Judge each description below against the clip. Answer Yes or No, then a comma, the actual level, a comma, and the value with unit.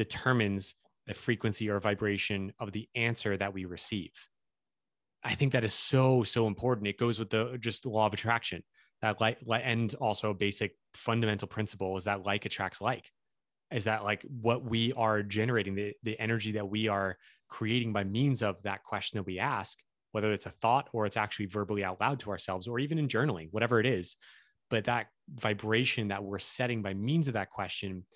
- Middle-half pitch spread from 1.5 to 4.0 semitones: Yes, narrow, 2.6 semitones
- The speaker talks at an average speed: Yes, average, 195 wpm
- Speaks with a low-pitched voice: Yes, low, 110 Hz